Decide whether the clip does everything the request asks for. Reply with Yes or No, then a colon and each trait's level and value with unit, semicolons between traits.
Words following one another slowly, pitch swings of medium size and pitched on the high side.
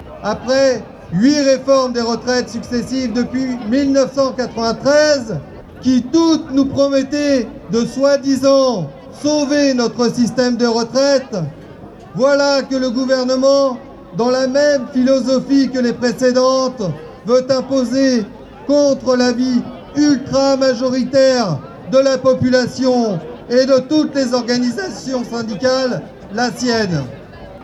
No: slow, 100 wpm; narrow, 2.2 semitones; very high, 255 Hz